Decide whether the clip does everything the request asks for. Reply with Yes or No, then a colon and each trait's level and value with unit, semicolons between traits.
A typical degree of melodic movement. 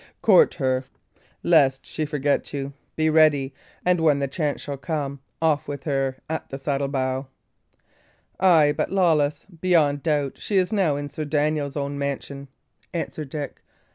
No: narrow, 2.3 semitones